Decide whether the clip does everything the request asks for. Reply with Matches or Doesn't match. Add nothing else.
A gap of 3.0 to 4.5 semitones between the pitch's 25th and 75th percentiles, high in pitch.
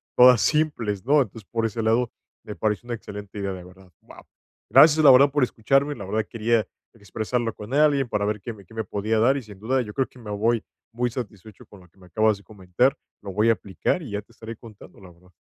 Doesn't match